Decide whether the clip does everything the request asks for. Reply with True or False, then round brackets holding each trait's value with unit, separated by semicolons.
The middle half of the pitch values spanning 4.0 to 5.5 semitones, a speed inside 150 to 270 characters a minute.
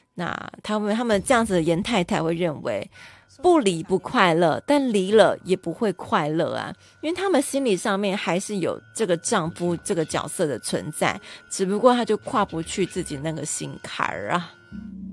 True (4.5 semitones; 265 characters per minute)